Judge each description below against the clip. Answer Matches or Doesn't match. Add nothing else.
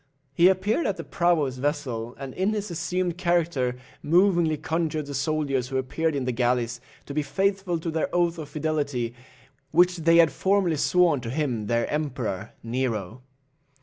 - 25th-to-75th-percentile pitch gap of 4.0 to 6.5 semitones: Matches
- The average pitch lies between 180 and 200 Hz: Doesn't match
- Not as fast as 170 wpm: Doesn't match